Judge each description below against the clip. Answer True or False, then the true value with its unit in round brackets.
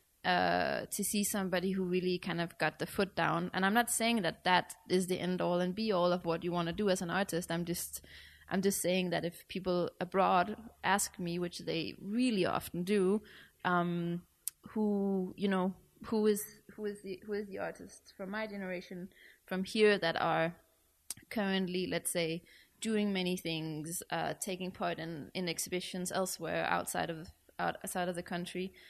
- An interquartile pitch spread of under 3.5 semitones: True (2.5 semitones)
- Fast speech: False (185 wpm)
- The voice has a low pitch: False (185 Hz)